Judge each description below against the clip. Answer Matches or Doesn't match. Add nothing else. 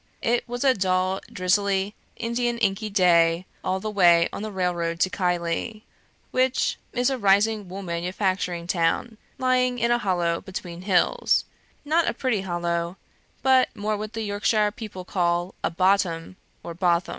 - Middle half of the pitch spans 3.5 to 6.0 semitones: Matches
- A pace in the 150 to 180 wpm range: Matches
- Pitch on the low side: Doesn't match